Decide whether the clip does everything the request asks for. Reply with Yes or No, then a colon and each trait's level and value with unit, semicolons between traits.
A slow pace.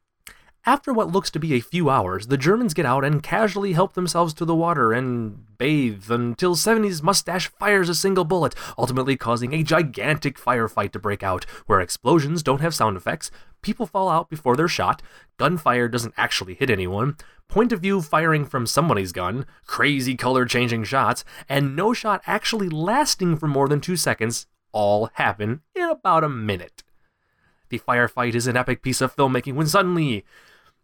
No: average, 175 wpm